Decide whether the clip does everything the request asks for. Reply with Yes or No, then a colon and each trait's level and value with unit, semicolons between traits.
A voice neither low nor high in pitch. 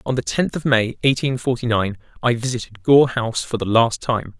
No: low, 120 Hz